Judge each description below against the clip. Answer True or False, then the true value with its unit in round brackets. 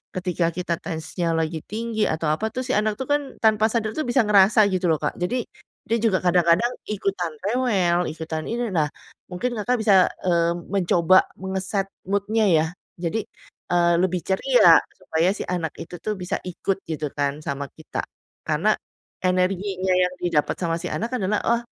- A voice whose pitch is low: False (185 Hz)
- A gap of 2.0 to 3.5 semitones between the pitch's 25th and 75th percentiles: False (4.0 semitones)